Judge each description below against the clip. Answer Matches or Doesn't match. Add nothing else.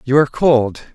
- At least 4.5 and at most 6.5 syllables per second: Matches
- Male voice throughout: Matches